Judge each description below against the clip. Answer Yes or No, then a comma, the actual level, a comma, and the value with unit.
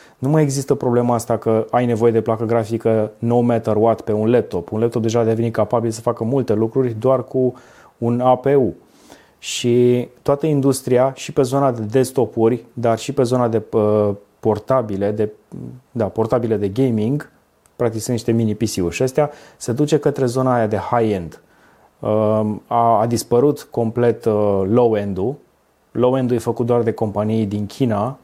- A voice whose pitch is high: No, low, 115 Hz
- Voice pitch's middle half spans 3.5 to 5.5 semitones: No, narrow, 2.4 semitones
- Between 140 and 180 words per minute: Yes, average, 165 wpm